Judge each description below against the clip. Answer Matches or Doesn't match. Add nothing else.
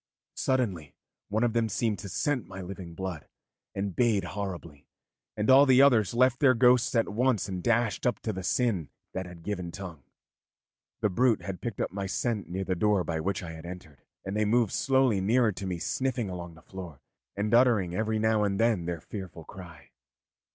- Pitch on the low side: Matches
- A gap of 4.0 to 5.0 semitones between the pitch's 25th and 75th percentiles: Matches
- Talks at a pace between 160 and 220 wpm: Matches